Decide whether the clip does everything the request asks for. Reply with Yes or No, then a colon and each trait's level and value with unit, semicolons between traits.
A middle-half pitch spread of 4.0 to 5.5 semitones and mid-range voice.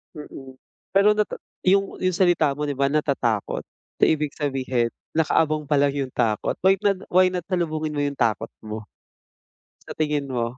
Yes: average, 4.5 semitones; medium, 150 Hz